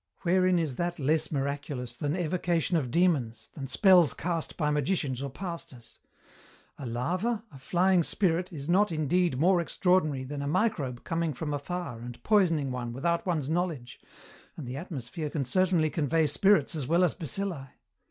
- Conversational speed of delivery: Yes, average, 160 wpm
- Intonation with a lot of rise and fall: No, average, 4.5 semitones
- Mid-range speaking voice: Yes, medium, 160 Hz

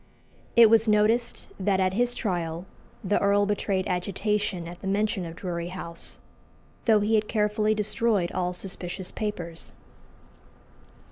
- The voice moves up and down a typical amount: Yes, average, 3.0 semitones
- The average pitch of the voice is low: No, high, 200 Hz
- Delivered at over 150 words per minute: No, slow, 135 wpm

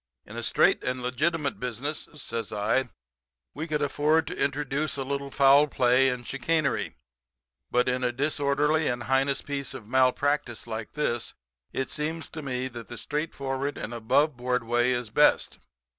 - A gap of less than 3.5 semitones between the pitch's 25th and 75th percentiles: Yes, average, 3.0 semitones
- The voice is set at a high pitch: No, low, 135 Hz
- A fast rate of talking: No, average, 160 wpm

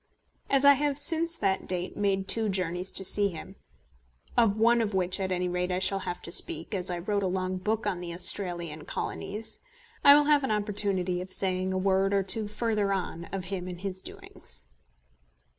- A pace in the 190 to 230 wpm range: Yes, average, 200 wpm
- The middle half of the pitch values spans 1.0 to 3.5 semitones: Yes, average, 2.7 semitones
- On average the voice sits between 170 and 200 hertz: Yes, high, 190 Hz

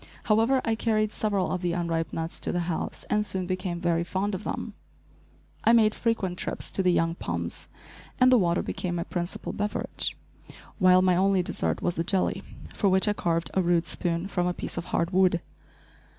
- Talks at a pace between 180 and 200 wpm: Yes, average, 195 wpm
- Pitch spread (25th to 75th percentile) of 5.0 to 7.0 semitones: No, average, 3.0 semitones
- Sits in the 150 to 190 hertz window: Yes, medium, 185 Hz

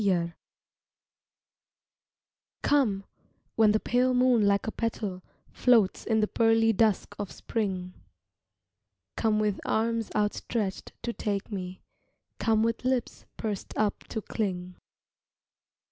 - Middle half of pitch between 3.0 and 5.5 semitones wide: No, narrow, 2.5 semitones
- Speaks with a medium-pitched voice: No, high, 215 Hz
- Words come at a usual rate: No, slow, 115 wpm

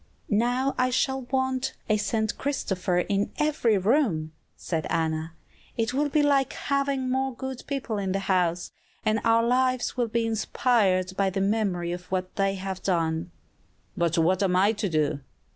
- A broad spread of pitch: Yes, wide, 5.8 semitones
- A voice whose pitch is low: No, high, 210 Hz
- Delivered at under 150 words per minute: No, average, 165 wpm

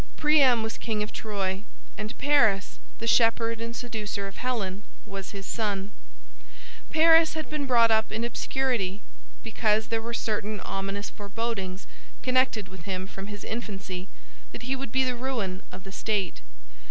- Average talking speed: Yes, average, 155 wpm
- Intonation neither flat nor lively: Yes, average, 3.5 semitones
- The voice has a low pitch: No, high, 220 Hz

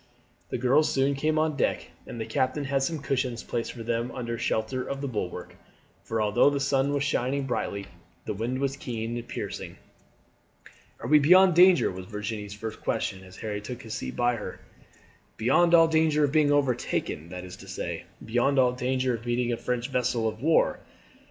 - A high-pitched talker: No, low, 125 Hz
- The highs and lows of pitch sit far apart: No, average, 3.9 semitones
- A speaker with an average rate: Yes, average, 190 wpm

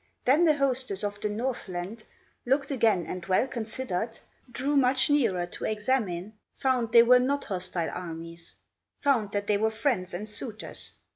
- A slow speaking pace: No, average, 155 wpm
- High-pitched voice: Yes, high, 220 Hz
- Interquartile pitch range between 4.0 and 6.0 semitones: Yes, wide, 5.6 semitones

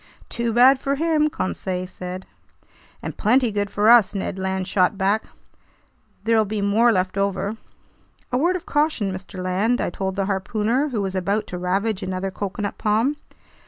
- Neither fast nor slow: Yes, average, 165 wpm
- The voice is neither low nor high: No, high, 205 Hz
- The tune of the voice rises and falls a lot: No, average, 3.8 semitones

